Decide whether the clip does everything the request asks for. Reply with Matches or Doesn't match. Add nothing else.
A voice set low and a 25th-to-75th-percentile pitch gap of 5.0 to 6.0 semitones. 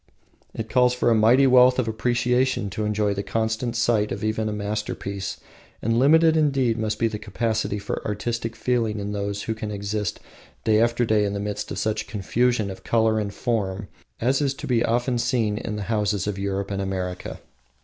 Doesn't match